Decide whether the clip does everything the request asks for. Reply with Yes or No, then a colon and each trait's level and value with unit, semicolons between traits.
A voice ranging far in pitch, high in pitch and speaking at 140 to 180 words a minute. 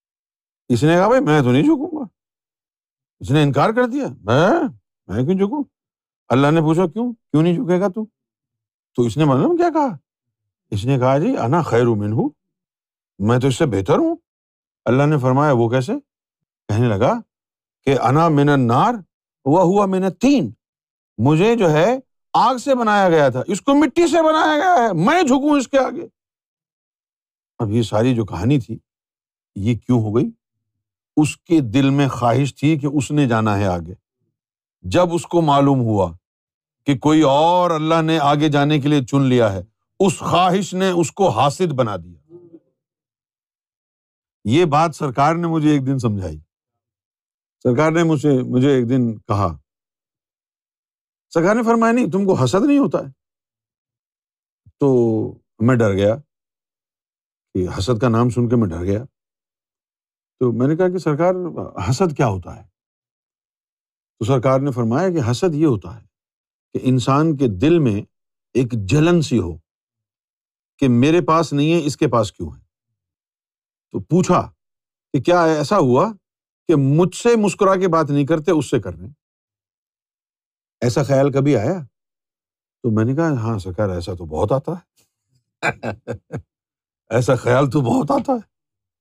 No: wide, 6.8 semitones; low, 135 Hz; average, 160 wpm